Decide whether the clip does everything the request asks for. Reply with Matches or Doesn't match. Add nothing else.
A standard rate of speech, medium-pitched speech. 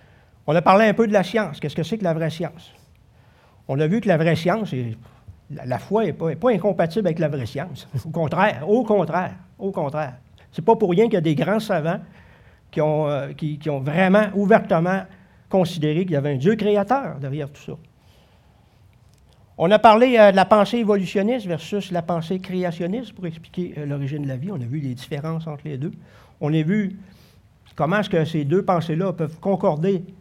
Matches